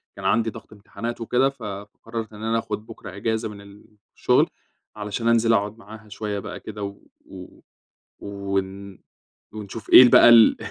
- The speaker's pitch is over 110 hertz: No, low, 105 Hz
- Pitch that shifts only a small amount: Yes, narrow, 2.2 semitones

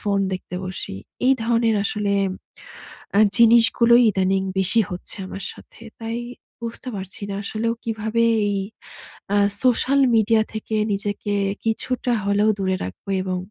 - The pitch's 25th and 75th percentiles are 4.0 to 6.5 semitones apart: No, average, 2.8 semitones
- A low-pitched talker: No, high, 215 Hz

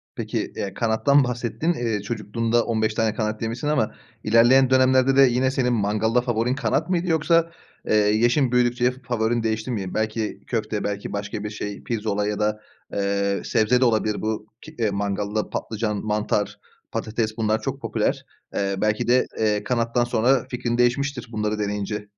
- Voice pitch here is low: Yes, low, 110 Hz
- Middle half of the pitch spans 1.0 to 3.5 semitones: Yes, average, 2.8 semitones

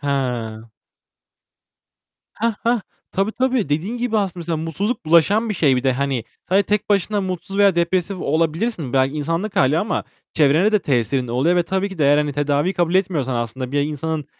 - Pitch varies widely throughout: Yes, wide, 5.8 semitones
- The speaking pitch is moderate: Yes, medium, 165 Hz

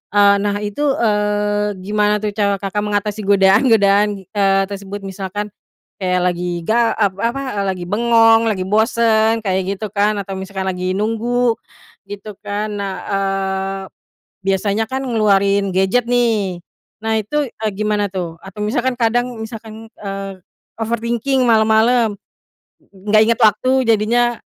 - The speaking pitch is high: Yes, high, 210 Hz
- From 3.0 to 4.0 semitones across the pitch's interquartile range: No, narrow, 2.4 semitones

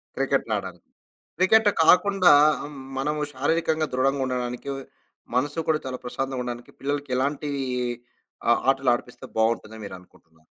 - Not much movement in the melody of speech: No, average, 3.7 semitones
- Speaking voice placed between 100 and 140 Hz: Yes, low, 135 Hz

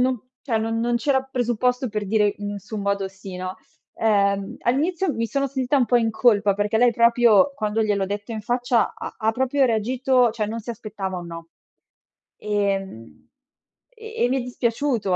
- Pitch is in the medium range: No, high, 225 Hz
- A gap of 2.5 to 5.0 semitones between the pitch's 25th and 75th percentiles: Yes, average, 3.5 semitones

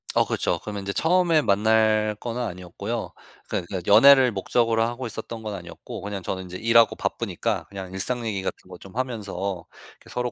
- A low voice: Yes, low, 110 Hz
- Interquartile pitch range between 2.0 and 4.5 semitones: Yes, average, 3.6 semitones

